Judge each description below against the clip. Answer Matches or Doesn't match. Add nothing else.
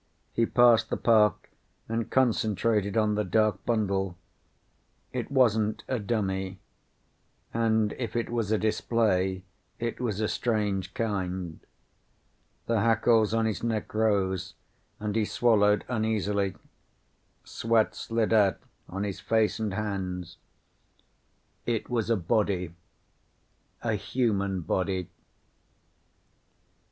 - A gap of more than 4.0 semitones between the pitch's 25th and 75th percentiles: Doesn't match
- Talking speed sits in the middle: Doesn't match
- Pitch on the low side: Matches